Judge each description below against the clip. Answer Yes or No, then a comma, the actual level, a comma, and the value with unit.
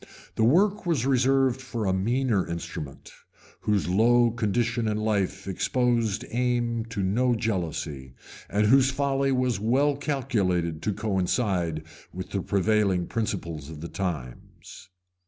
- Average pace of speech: No, slow, 130 wpm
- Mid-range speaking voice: No, low, 110 Hz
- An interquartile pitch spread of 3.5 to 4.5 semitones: No, average, 5.1 semitones